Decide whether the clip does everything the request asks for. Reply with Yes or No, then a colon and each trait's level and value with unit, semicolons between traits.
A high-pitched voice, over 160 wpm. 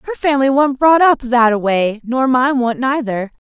Yes: very high, 250 Hz; fast, 205 wpm